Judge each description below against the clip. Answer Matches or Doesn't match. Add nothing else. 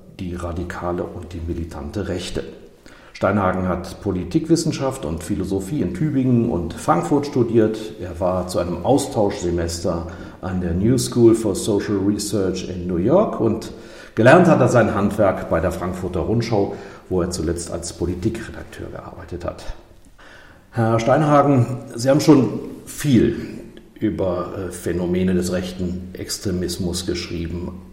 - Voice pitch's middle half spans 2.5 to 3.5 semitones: Doesn't match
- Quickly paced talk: Doesn't match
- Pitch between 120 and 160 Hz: Doesn't match